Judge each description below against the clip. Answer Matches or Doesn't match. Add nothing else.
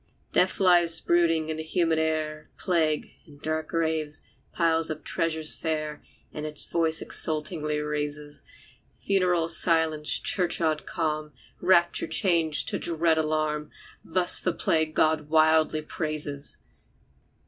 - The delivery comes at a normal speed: Doesn't match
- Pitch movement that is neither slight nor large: Doesn't match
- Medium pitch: Matches